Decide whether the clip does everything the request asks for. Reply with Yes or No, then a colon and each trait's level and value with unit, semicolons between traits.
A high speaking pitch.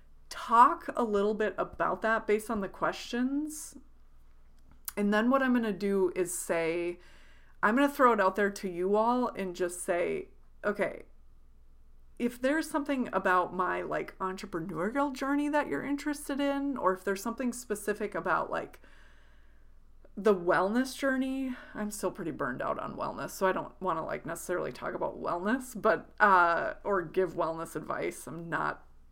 Yes: high, 200 Hz